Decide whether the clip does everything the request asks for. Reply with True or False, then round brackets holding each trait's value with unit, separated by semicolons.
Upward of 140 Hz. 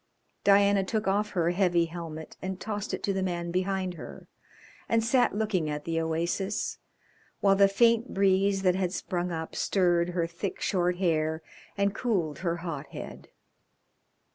True (185 Hz)